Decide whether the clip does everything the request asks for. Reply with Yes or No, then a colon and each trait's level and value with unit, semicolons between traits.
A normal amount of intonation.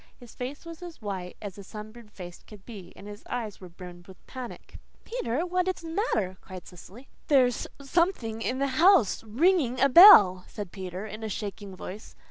No: wide, 6.5 semitones